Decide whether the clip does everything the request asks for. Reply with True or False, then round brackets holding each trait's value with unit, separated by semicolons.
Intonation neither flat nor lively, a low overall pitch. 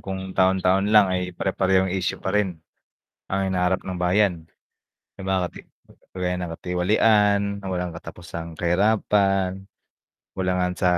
False (1.4 semitones; 95 Hz)